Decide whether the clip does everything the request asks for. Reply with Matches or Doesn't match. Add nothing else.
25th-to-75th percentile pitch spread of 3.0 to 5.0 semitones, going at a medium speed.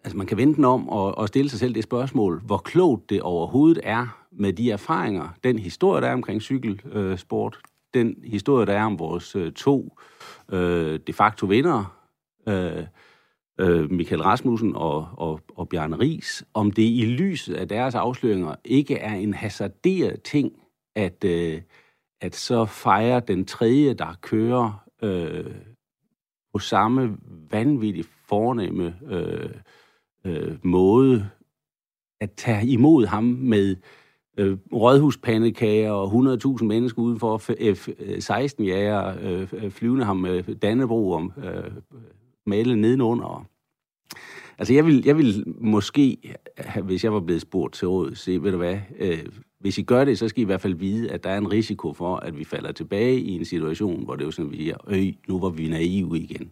Matches